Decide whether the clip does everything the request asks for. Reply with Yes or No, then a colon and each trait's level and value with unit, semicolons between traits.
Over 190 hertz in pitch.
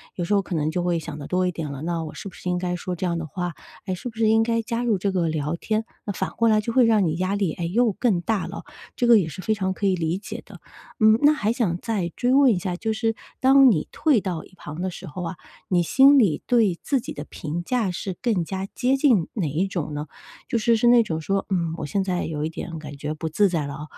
No: medium, 185 Hz